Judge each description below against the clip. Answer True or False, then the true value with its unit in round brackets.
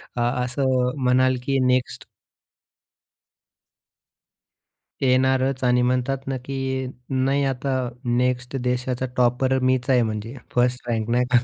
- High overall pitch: False (125 Hz)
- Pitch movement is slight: True (1.2 semitones)